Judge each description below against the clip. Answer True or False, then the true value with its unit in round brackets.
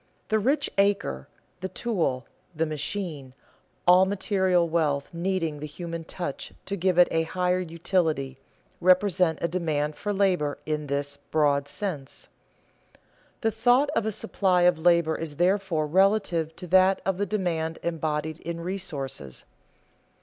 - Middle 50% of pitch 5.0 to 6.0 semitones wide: False (3.8 semitones)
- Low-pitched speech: False (170 Hz)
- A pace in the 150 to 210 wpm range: False (140 wpm)